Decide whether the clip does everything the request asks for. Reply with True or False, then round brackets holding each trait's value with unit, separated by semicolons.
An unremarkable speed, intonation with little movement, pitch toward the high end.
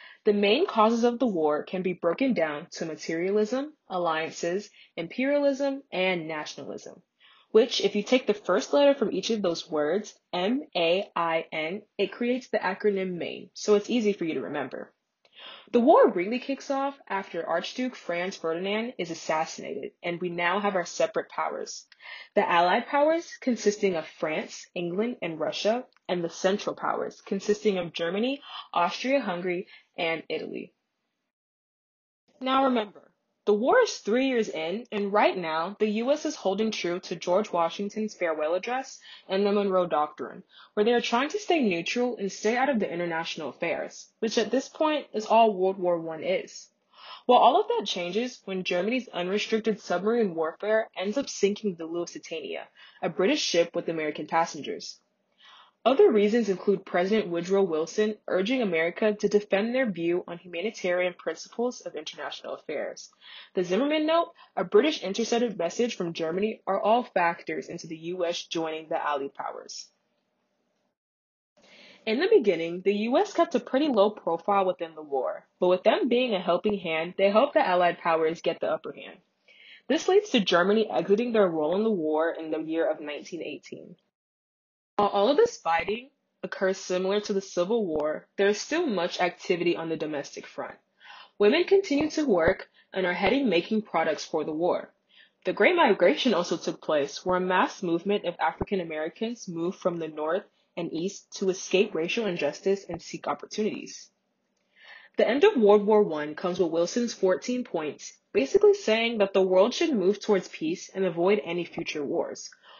False (165 wpm; 5.3 semitones; 195 Hz)